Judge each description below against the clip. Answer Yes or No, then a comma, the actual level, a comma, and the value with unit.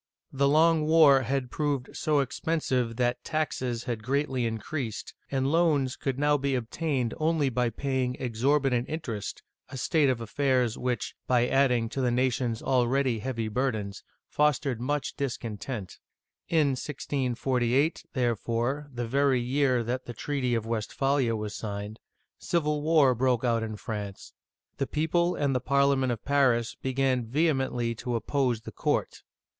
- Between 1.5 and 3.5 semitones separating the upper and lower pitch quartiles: Yes, average, 3.0 semitones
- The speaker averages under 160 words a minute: Yes, average, 145 wpm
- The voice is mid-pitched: No, low, 130 Hz